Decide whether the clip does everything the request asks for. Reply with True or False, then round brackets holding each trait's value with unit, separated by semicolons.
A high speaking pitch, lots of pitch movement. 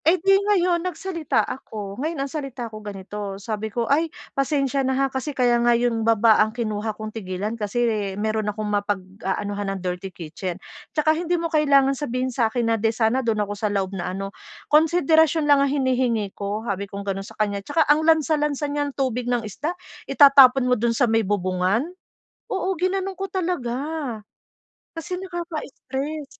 True (245 Hz; 6.2 semitones)